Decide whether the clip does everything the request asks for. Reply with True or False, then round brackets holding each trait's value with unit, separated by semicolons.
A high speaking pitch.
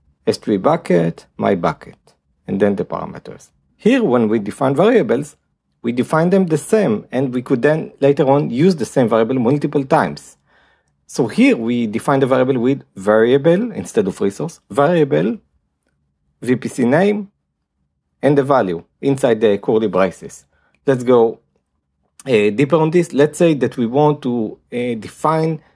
False (135 Hz)